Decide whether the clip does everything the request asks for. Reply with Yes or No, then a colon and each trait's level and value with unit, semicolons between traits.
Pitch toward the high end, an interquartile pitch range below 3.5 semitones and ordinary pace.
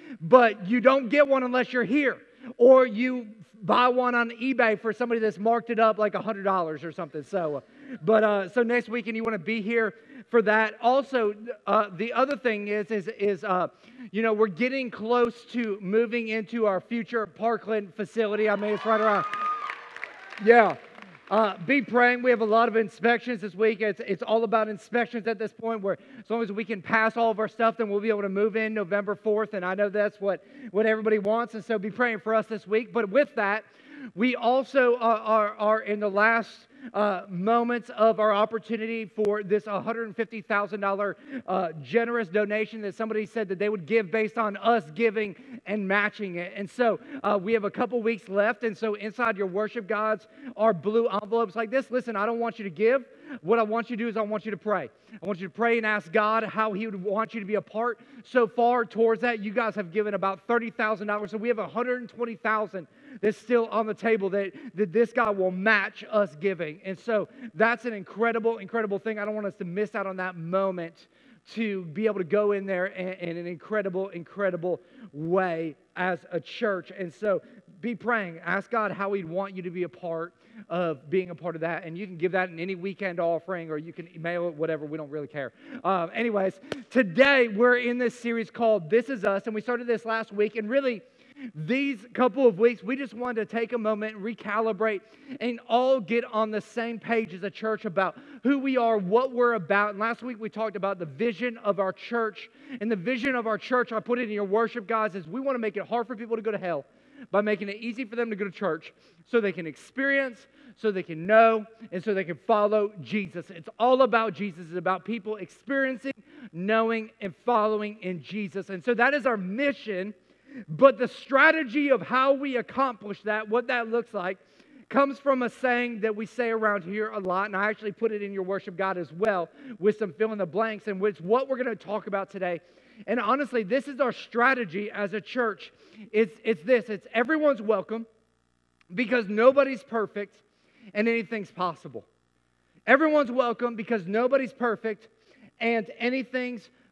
No: high, 220 Hz; average, 2.8 semitones; fast, 210 wpm